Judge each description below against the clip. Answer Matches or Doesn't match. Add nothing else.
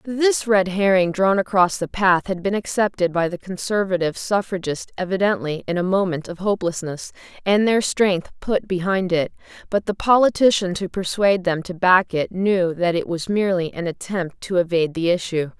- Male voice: Doesn't match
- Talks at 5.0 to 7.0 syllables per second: Matches